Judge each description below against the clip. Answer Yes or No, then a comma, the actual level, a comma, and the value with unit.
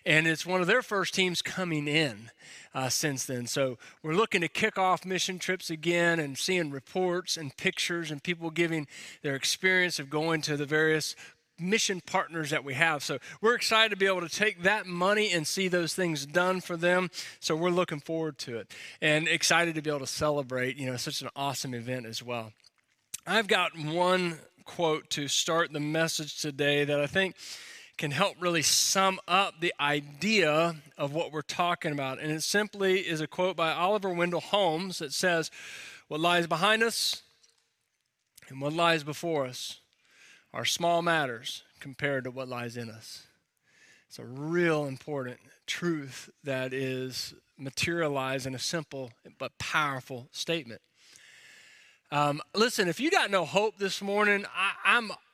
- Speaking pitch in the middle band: Yes, medium, 165 Hz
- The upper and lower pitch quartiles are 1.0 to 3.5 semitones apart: No, average, 4.3 semitones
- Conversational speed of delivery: Yes, average, 170 wpm